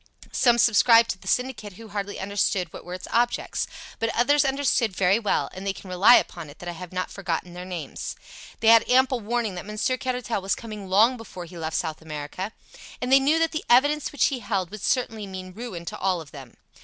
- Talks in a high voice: Yes, high, 205 Hz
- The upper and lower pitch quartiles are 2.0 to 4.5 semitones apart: No, average, 4.9 semitones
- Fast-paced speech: Yes, fast, 220 wpm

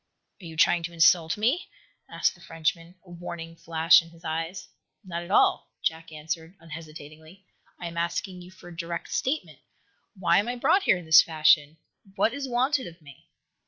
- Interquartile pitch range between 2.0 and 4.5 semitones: Yes, narrow, 2.4 semitones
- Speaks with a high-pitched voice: No, medium, 170 Hz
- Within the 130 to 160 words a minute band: No, average, 185 wpm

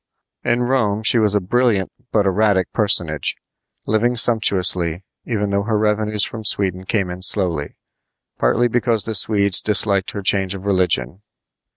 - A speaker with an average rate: Yes, average, 150 wpm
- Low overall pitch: Yes, low, 100 Hz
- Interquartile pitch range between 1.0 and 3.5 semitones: Yes, average, 2.7 semitones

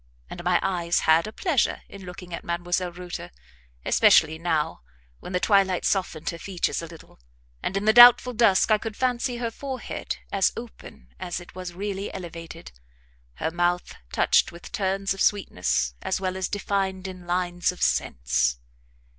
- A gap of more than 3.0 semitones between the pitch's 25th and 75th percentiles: No, average, 2.7 semitones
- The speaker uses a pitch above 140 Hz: Yes, medium, 185 Hz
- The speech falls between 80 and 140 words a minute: No, average, 165 wpm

